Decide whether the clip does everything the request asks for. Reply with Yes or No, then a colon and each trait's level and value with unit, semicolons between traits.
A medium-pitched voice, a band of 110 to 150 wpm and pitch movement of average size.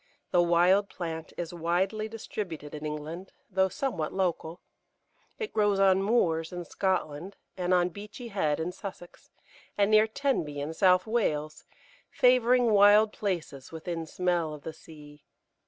Yes: medium, 180 Hz; average, 140 wpm; average, 4.2 semitones